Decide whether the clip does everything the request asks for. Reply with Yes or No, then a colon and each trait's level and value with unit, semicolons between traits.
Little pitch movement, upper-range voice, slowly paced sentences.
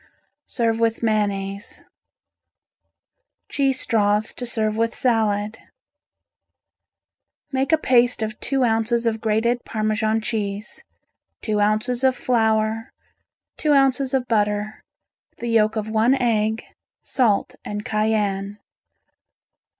Yes: narrow, 2.1 semitones; high, 220 Hz; slow, 105 wpm